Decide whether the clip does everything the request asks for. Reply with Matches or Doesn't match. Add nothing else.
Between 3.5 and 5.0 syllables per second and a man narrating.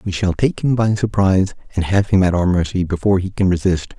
Doesn't match